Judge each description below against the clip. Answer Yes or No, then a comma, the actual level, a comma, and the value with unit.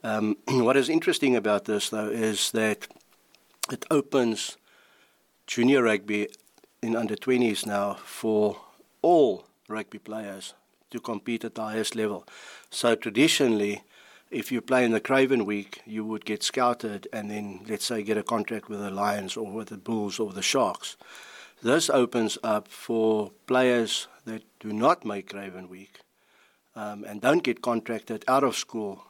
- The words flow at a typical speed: Yes, average, 155 wpm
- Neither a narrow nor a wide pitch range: No, narrow, 1.8 semitones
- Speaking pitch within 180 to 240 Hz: No, low, 110 Hz